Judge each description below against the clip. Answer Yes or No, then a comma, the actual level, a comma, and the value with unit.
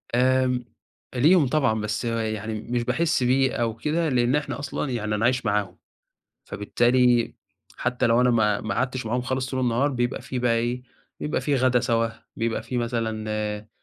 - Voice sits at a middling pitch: No, low, 120 Hz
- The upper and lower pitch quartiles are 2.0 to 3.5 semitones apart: Yes, narrow, 2.4 semitones